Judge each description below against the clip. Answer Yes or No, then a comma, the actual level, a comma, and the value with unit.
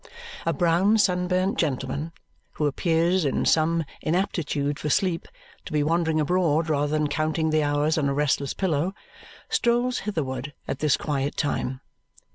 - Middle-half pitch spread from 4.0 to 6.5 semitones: No, average, 3.2 semitones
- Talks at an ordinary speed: Yes, average, 145 wpm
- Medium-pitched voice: Yes, medium, 155 Hz